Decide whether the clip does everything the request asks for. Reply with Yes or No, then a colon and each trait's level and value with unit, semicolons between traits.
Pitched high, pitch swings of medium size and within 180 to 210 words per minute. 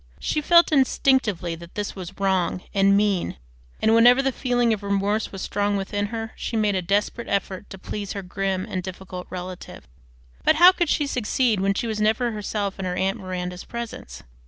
Yes: high, 205 Hz; average, 3.5 semitones; average, 190 wpm